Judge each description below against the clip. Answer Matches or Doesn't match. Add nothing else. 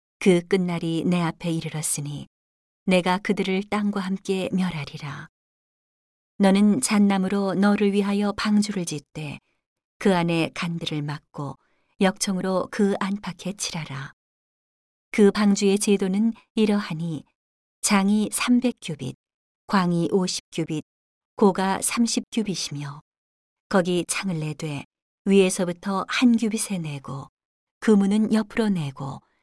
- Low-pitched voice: Doesn't match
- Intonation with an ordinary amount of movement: Matches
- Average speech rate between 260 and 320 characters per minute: Doesn't match